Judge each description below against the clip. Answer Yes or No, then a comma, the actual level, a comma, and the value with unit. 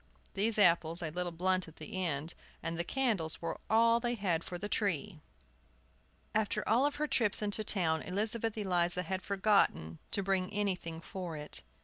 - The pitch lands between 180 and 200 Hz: Yes, medium, 185 Hz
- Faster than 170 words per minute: No, average, 165 wpm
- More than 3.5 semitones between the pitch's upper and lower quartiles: Yes, average, 4.0 semitones